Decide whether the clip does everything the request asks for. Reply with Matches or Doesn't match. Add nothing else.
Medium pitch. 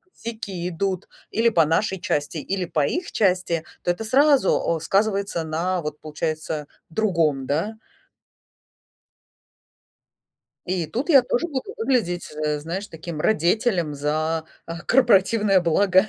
Matches